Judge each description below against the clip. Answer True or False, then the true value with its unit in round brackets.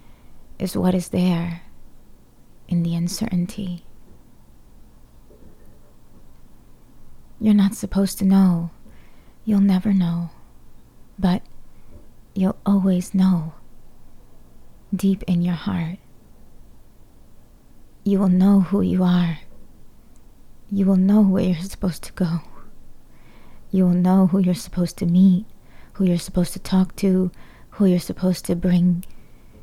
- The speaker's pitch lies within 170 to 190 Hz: True (185 Hz)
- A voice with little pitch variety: True (1.8 semitones)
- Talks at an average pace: False (115 wpm)